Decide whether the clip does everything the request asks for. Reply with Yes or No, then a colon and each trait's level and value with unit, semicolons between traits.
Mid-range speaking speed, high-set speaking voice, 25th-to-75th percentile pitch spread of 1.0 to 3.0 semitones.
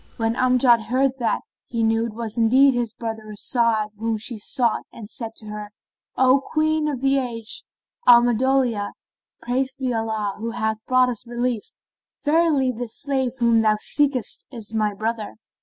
Yes: average, 160 wpm; high, 235 Hz; average, 2.7 semitones